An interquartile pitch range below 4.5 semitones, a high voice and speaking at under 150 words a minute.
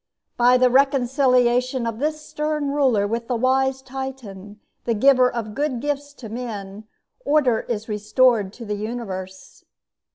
Yes: average, 3.6 semitones; high, 245 Hz; average, 140 wpm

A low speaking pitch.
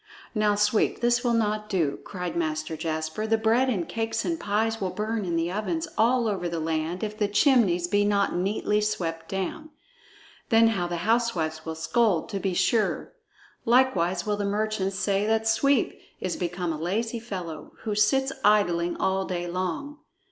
No: high, 205 Hz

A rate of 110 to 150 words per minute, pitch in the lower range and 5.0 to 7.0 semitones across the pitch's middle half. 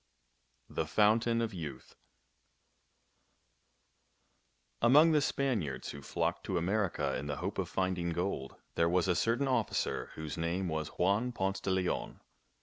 Yes: average, 140 wpm; very low, 95 Hz; wide, 5.5 semitones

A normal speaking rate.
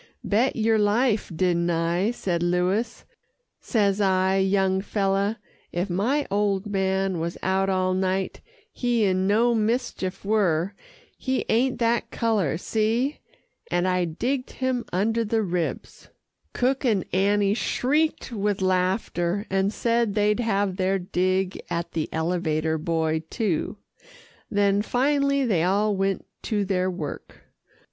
No: slow, 130 wpm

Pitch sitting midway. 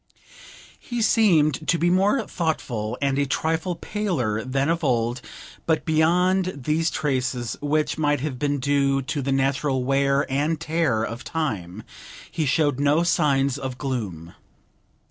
Yes: medium, 145 Hz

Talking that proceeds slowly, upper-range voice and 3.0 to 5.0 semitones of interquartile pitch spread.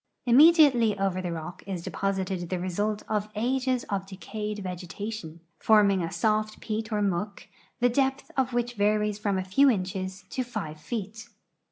No: average, 165 wpm; high, 210 Hz; average, 3.6 semitones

